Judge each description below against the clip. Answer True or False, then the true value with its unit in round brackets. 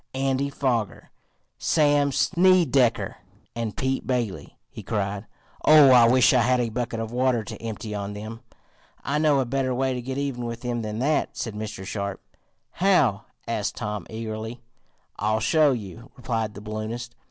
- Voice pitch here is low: True (120 Hz)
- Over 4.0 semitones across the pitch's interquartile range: False (3.5 semitones)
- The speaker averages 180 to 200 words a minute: False (165 wpm)